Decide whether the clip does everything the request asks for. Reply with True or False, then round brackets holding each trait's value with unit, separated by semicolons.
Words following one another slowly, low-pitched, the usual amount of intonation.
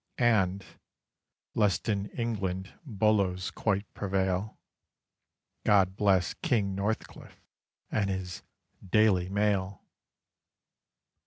False (80 wpm; 100 Hz; 2.2 semitones)